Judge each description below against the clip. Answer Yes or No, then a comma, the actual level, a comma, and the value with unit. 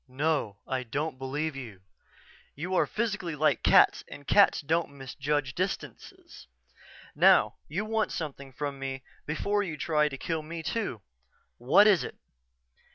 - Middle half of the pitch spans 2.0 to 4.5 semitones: Yes, average, 4.1 semitones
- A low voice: No, medium, 150 Hz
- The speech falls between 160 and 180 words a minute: No, average, 145 wpm